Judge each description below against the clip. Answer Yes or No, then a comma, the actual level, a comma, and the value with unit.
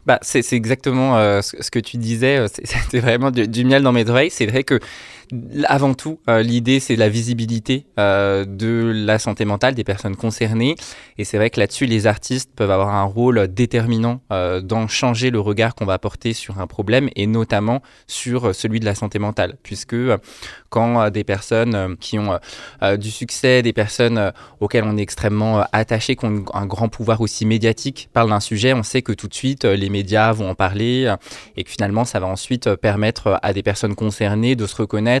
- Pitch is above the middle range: No, low, 115 Hz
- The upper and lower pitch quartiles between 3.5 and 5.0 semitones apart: No, average, 2.8 semitones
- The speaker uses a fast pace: No, average, 195 wpm